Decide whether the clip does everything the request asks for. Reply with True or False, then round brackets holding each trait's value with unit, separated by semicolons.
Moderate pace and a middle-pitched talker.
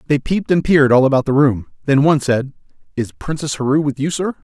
False (225 wpm; 145 Hz)